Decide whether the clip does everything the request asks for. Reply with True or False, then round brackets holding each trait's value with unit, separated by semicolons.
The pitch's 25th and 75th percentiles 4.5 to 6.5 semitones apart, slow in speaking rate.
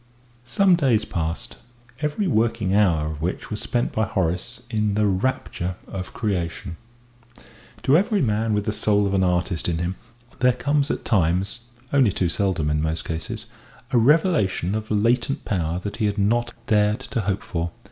False (4.9 semitones; 170 wpm)